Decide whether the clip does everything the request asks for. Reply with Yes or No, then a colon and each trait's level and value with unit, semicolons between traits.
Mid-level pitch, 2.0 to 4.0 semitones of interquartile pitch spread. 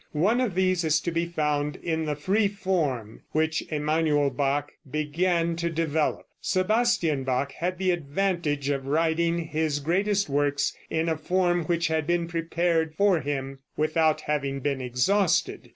Yes: medium, 160 Hz; average, 3.1 semitones